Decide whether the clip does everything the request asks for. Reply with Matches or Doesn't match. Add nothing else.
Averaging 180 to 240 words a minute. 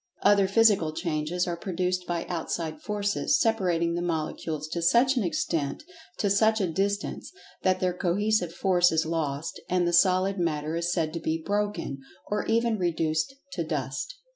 Doesn't match